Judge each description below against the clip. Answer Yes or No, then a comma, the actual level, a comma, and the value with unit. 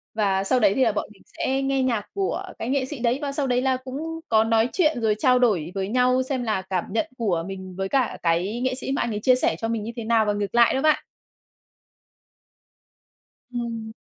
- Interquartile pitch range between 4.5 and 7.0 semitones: No, average, 3.8 semitones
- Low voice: No, high, 235 Hz